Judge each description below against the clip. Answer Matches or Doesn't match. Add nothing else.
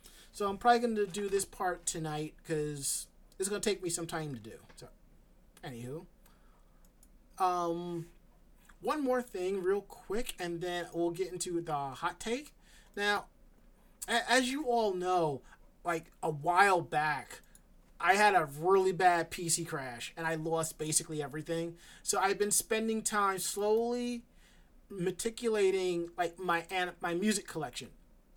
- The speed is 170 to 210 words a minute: Doesn't match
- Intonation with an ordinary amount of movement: Matches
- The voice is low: Doesn't match